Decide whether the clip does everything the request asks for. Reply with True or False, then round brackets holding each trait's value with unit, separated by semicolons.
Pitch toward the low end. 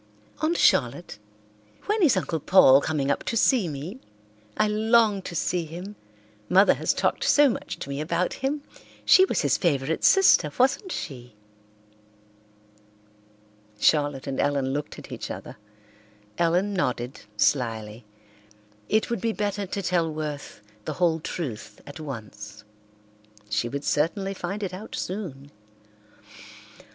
False (170 Hz)